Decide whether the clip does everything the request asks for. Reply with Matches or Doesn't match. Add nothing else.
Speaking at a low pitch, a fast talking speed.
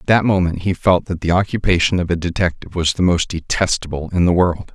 Matches